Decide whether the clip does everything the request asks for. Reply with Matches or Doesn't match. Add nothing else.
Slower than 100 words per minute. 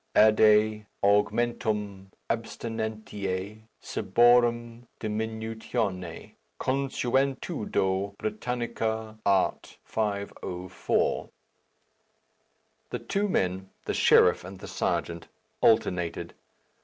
Matches